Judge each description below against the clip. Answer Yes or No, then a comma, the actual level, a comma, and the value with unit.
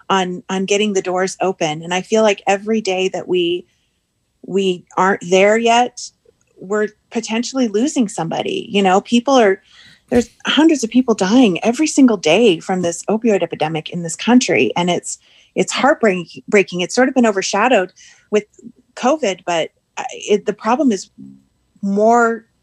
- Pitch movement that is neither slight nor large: Yes, average, 4.1 semitones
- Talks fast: No, average, 155 wpm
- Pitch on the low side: No, high, 205 Hz